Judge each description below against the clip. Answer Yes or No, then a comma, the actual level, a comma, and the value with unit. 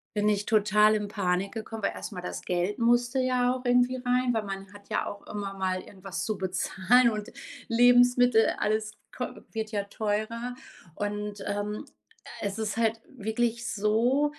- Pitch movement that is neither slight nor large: Yes, average, 3.0 semitones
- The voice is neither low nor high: No, high, 215 Hz